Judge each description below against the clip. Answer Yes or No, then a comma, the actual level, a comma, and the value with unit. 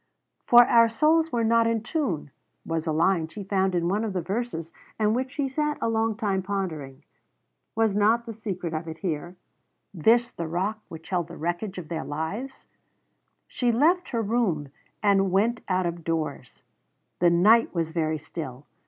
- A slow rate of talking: No, average, 180 wpm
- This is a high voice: Yes, high, 195 Hz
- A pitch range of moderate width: No, wide, 5.7 semitones